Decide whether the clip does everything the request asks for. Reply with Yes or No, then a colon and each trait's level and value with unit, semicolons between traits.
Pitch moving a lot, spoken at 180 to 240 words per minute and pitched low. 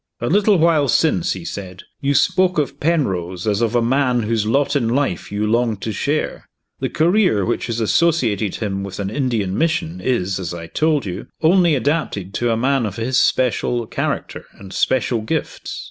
Yes: wide, 6.6 semitones; average, 185 wpm; low, 120 Hz